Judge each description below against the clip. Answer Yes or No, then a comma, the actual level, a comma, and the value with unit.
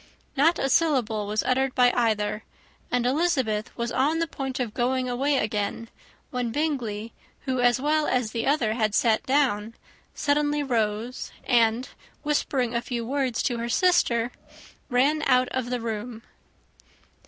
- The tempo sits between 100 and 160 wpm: Yes, average, 150 wpm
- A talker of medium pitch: No, very high, 250 Hz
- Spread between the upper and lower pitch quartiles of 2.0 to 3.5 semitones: Yes, average, 3.1 semitones